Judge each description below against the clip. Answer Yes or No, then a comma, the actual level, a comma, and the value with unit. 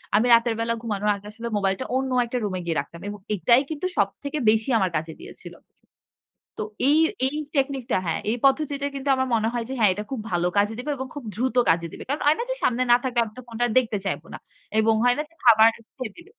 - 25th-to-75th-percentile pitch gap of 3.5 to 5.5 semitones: Yes, average, 4.3 semitones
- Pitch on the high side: Yes, high, 230 Hz